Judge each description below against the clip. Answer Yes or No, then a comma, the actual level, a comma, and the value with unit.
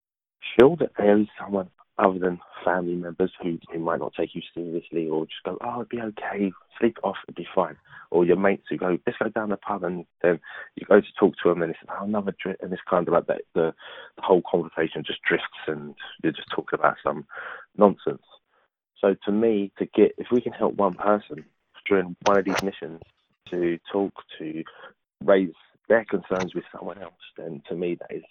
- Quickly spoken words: Yes, fast, 210 wpm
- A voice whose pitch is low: Yes, very low, 95 Hz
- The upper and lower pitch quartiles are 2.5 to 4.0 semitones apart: Yes, average, 2.8 semitones